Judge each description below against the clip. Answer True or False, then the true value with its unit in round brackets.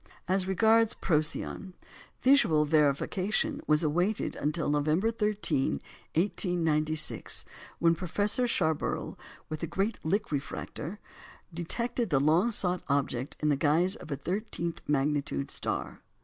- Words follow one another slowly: True (120 wpm)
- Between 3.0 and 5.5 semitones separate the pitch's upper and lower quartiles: True (5.1 semitones)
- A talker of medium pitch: True (170 Hz)